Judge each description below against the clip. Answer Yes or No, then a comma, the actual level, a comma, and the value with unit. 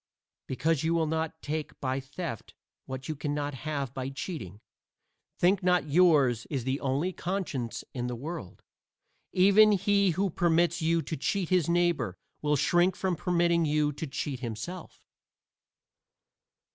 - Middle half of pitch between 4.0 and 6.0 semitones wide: Yes, average, 4.4 semitones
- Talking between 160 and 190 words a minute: No, average, 145 wpm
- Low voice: No, medium, 155 Hz